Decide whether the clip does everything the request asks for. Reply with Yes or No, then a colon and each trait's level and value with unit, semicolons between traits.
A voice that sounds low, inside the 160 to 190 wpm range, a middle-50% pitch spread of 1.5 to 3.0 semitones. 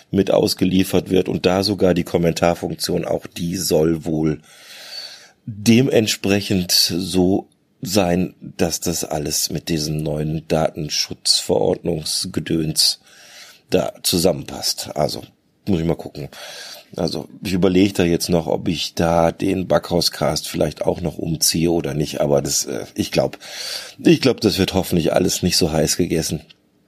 No: very low, 85 Hz; average, 135 wpm; average, 2.7 semitones